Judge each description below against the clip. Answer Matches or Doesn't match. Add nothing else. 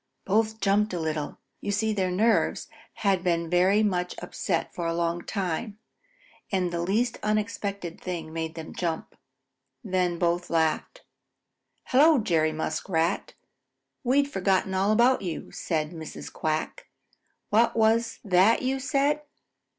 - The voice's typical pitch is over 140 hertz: Matches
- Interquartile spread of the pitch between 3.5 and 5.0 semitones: Matches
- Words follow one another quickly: Doesn't match